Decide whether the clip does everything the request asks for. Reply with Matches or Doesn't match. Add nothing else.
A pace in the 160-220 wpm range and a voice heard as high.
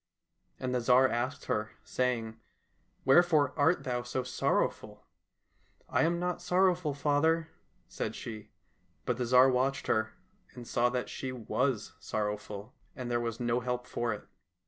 Doesn't match